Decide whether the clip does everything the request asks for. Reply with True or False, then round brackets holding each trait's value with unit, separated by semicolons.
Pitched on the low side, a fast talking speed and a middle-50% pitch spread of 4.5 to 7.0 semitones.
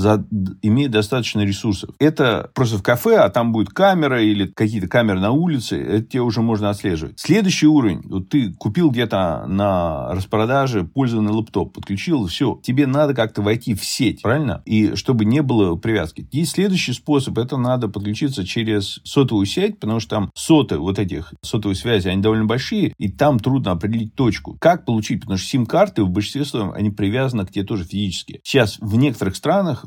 True (110 Hz; 180 wpm; 4.8 semitones)